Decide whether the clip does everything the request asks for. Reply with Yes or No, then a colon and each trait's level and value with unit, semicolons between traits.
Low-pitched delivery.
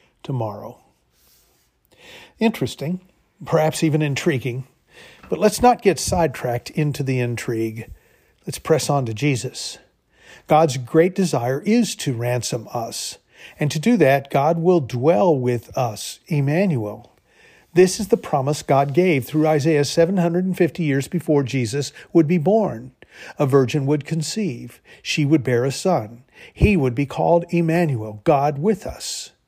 No: medium, 150 Hz